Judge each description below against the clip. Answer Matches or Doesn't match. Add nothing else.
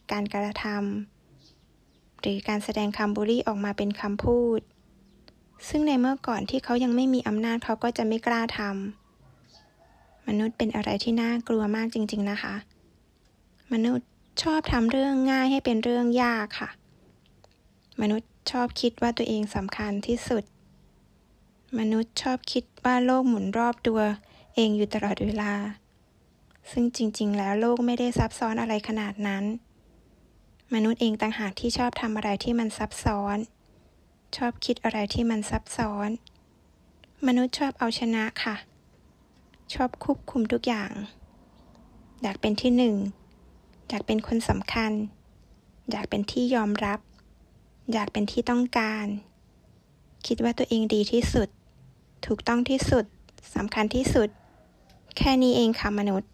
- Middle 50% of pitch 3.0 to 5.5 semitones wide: Doesn't match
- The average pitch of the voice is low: Doesn't match